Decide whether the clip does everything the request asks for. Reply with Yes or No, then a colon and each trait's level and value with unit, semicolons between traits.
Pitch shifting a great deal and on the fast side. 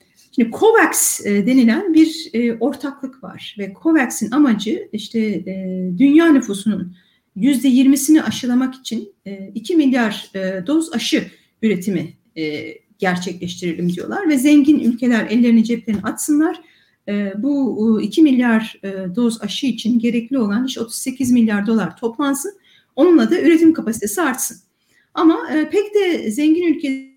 No: wide, 5.9 semitones; average, 115 wpm